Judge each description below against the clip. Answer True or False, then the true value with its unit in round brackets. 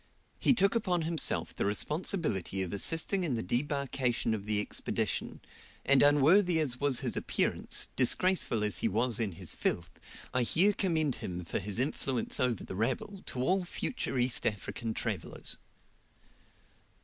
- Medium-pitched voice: False (130 Hz)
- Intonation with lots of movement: True (7.0 semitones)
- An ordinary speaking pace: True (150 wpm)